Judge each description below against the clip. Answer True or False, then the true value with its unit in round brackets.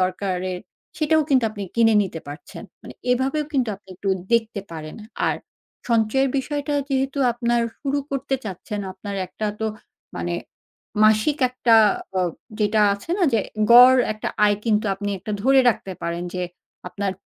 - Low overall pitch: False (220 Hz)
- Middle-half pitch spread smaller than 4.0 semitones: False (5.0 semitones)